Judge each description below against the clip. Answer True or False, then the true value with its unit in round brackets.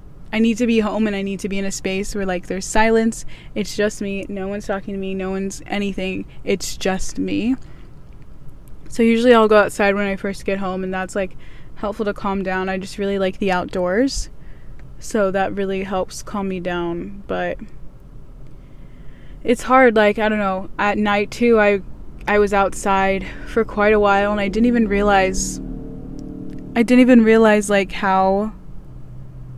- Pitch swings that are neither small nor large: False (2.0 semitones)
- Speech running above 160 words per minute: True (185 wpm)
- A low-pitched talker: False (200 Hz)